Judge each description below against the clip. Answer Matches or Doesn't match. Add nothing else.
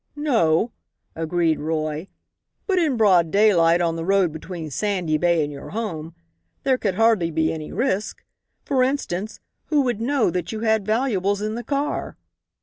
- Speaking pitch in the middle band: Doesn't match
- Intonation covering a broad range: Matches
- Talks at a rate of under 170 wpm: Matches